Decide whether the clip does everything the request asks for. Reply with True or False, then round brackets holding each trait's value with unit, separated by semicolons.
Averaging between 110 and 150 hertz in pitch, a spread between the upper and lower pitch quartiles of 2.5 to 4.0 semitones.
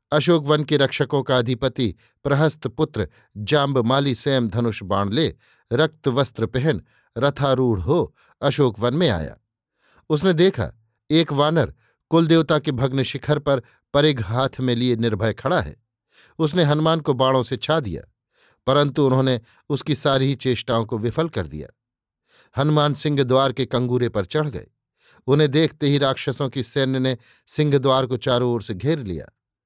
True (135 Hz; 3.6 semitones)